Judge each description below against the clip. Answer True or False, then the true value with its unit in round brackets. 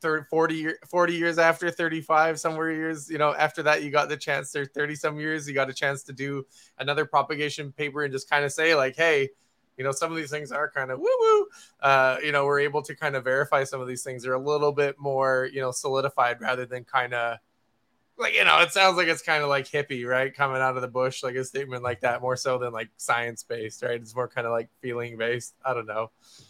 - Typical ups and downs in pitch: True (3.4 semitones)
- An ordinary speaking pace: False (250 wpm)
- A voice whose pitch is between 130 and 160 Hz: True (140 Hz)